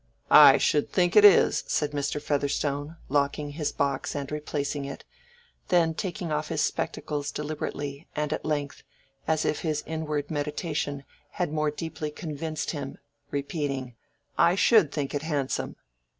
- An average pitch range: No, narrow, 1.8 semitones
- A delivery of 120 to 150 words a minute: Yes, average, 145 wpm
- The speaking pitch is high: No, medium, 150 Hz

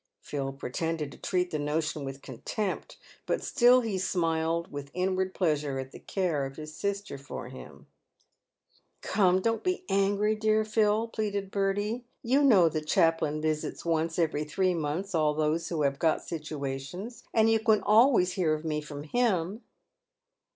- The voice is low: No, medium, 170 Hz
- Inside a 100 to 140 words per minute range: No, average, 165 wpm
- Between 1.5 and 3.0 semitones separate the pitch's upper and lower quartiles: No, average, 5.3 semitones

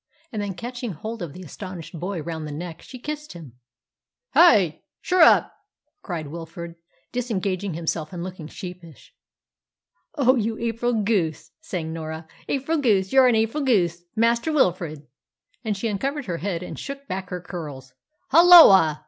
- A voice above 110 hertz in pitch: Yes, high, 190 Hz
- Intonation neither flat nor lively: No, wide, 6.3 semitones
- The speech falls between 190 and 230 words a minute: No, average, 150 wpm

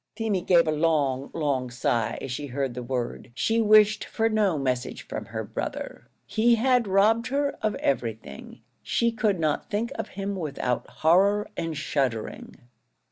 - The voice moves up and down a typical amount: No, wide, 8.2 semitones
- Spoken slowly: No, average, 160 wpm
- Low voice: No, medium, 170 Hz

